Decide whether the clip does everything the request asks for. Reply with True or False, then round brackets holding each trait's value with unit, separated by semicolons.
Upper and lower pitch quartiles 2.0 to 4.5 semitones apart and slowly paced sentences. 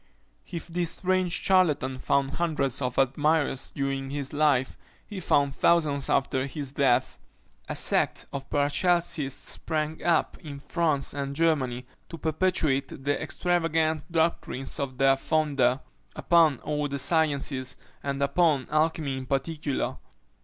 True (3.0 semitones; 130 wpm)